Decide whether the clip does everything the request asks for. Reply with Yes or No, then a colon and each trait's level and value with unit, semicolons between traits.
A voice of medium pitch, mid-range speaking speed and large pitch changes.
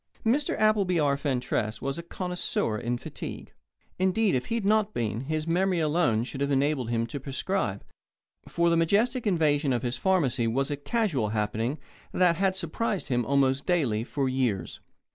Yes: medium, 145 Hz; average, 170 wpm; wide, 7.1 semitones